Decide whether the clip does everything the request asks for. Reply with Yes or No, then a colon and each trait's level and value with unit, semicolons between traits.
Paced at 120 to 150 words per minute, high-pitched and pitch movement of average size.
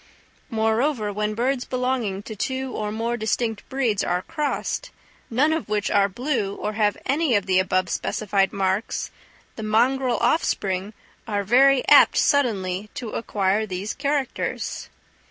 Yes: average, 140 wpm; high, 220 Hz; average, 4.4 semitones